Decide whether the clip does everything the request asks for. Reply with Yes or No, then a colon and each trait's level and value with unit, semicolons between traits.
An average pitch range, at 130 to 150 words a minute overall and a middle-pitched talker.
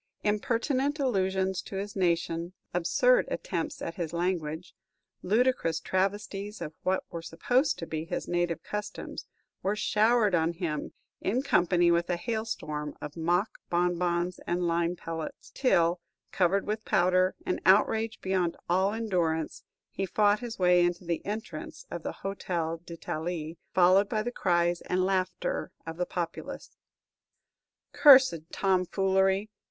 Yes: average, 3.3 semitones; slow, 135 wpm; medium, 180 Hz